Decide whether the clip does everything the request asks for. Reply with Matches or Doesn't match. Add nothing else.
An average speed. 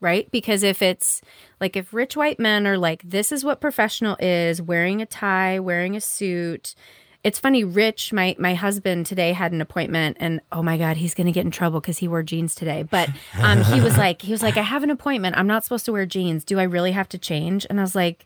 Doesn't match